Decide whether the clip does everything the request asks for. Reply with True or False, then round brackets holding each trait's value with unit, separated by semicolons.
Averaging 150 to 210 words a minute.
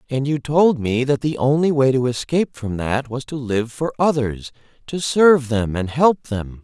True (200 wpm)